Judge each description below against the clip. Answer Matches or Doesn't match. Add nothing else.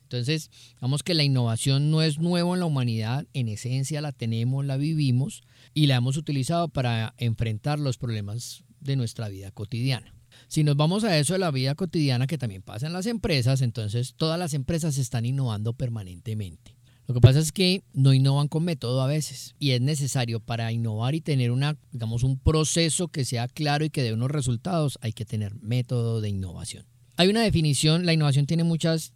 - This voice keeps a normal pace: Doesn't match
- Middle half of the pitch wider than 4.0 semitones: Matches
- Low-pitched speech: Matches